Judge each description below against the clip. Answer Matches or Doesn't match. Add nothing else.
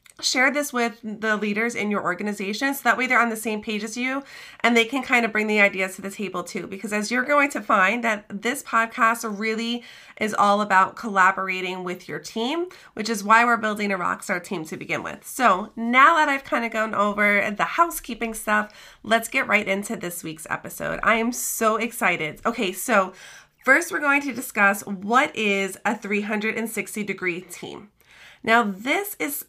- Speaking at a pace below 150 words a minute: Doesn't match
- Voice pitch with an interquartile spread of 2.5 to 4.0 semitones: Matches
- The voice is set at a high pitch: Matches